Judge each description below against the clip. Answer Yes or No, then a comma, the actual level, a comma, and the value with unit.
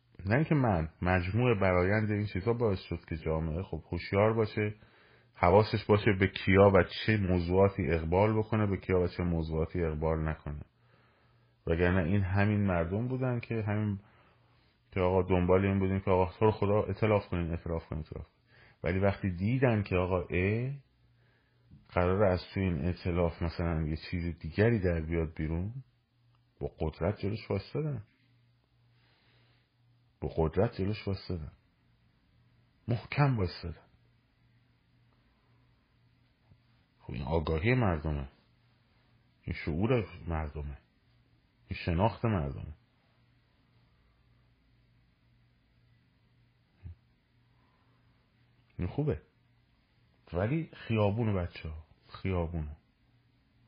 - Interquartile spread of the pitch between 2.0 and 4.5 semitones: No, average, 5.1 semitones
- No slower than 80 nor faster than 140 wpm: Yes, slow, 105 wpm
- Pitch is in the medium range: No, low, 105 Hz